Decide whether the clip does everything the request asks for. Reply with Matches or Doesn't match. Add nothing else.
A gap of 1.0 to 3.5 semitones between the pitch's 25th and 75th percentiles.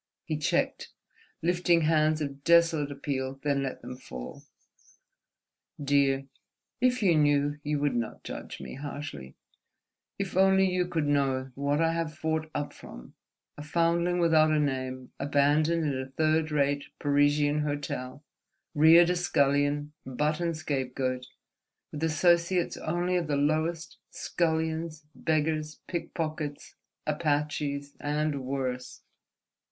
Matches